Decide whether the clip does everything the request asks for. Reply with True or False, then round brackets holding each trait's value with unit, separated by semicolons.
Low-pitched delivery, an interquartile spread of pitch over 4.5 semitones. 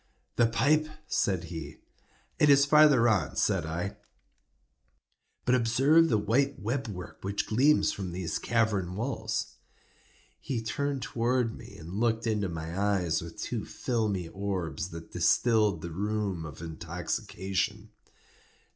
True (105 Hz; 5.1 semitones)